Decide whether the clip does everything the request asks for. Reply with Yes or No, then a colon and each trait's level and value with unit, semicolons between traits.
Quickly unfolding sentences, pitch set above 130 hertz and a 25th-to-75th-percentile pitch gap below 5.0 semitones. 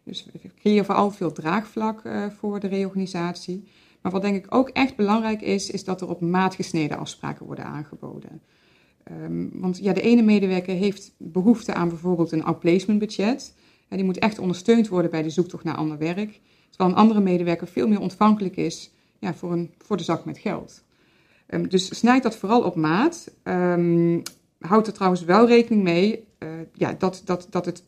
No: average, 185 wpm; medium, 185 Hz; average, 3.2 semitones